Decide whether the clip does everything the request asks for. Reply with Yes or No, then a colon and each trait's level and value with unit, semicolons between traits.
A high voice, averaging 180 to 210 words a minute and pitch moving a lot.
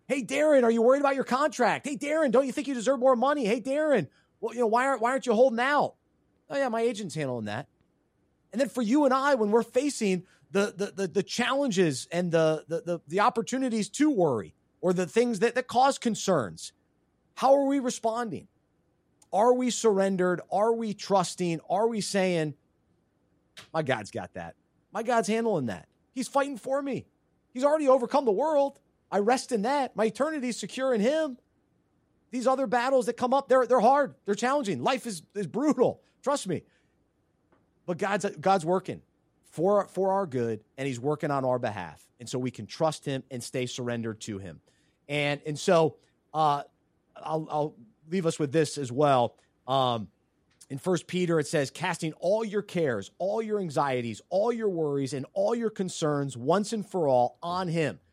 Yes: high, 200 Hz; average, 190 wpm; wide, 8.3 semitones